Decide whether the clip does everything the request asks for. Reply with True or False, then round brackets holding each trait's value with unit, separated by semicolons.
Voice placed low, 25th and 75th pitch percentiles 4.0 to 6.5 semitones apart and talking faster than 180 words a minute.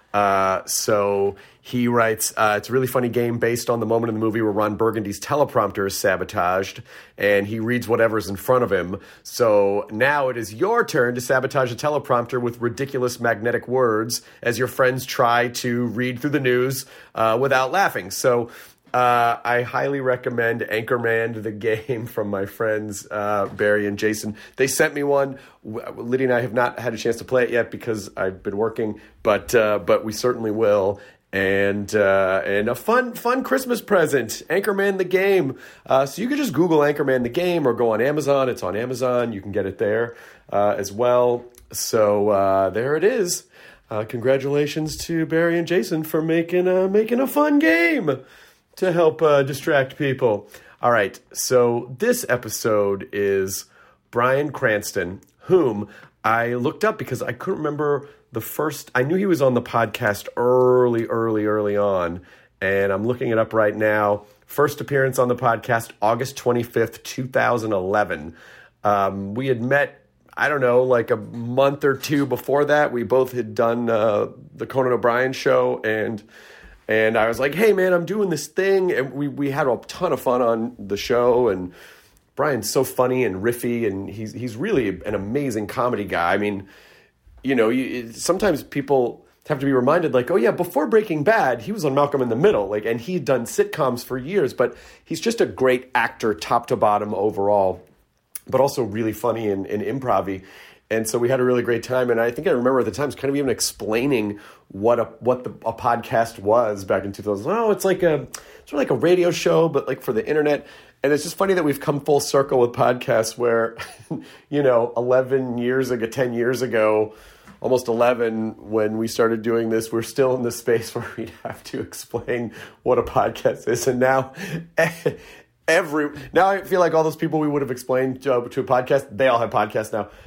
True (125 Hz; 4.3 semitones; 190 wpm)